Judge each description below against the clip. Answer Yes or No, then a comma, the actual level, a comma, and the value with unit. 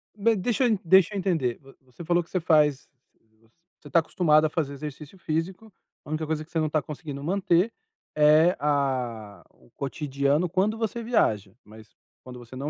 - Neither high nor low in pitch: Yes, medium, 155 Hz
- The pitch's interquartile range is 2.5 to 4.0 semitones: No, average, 4.7 semitones